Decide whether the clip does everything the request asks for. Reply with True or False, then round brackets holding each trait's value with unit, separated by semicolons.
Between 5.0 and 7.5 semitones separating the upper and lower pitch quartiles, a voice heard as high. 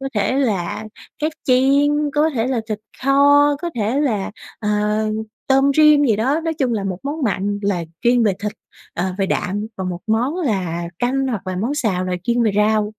True (5.6 semitones; 235 Hz)